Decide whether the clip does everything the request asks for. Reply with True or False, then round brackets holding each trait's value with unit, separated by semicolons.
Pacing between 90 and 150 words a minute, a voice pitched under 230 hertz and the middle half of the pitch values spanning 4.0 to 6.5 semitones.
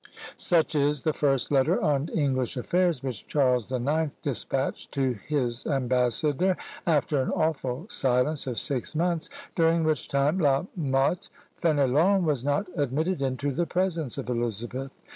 False (145 wpm; 140 Hz; 3.6 semitones)